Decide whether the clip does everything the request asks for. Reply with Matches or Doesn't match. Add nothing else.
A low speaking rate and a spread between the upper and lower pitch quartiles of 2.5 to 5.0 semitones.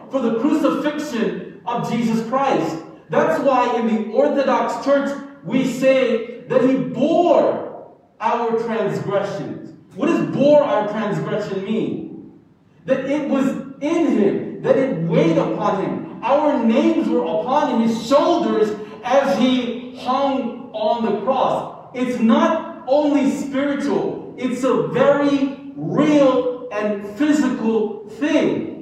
Matches